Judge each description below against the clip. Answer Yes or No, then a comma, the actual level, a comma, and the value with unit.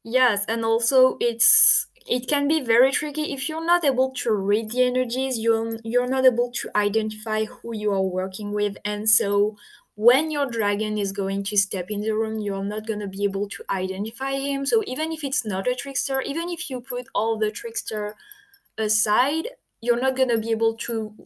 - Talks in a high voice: Yes, high, 230 Hz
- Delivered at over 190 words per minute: Yes, average, 200 wpm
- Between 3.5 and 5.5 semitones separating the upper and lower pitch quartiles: Yes, average, 4.1 semitones